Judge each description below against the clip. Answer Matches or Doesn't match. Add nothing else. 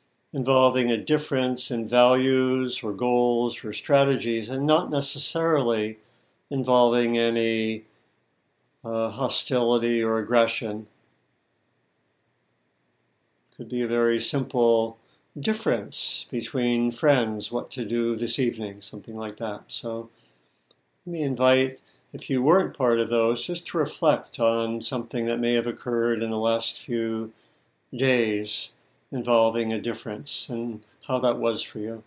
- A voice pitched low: Matches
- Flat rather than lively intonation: Matches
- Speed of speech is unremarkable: Doesn't match